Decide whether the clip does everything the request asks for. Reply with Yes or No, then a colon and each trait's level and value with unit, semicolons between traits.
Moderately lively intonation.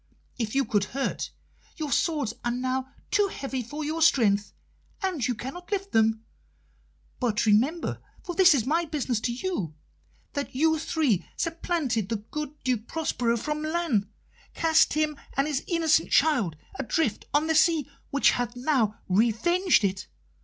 No: wide, 5.8 semitones